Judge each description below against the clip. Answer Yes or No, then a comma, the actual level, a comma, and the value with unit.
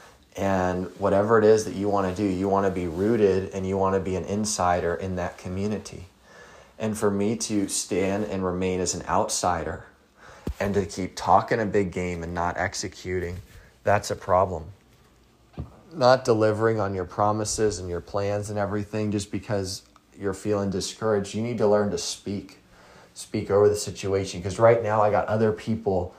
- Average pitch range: No, narrow, 2.3 semitones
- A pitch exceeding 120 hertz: No, low, 100 Hz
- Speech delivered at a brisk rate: No, average, 180 wpm